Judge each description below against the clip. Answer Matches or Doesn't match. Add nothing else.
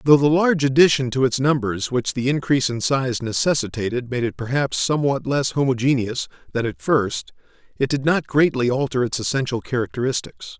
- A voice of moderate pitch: Doesn't match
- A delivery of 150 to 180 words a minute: Matches